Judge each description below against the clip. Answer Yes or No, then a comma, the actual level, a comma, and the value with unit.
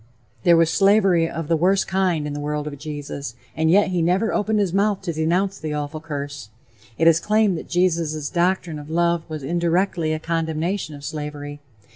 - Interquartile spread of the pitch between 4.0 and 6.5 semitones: No, average, 3.6 semitones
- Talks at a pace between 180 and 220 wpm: Yes, average, 190 wpm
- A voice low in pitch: No, medium, 165 Hz